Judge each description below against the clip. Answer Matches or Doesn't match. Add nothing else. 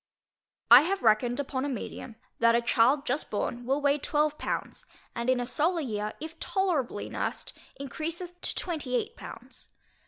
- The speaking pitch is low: Doesn't match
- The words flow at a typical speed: Matches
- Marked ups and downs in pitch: Doesn't match